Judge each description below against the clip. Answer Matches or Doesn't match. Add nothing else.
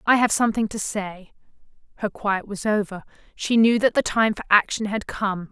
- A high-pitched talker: Matches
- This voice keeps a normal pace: Matches